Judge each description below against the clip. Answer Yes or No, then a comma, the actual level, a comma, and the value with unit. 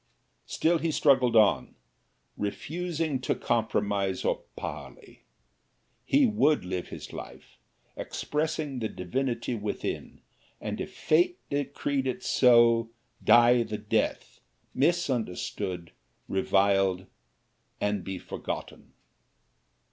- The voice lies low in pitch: Yes, low, 120 Hz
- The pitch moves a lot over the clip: Yes, wide, 6.5 semitones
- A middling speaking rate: No, slow, 95 wpm